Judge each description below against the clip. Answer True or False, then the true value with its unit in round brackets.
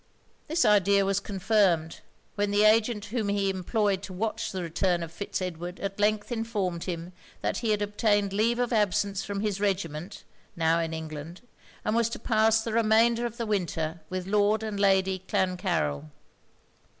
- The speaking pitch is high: True (200 Hz)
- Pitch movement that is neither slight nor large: True (3.0 semitones)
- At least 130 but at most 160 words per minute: False (170 wpm)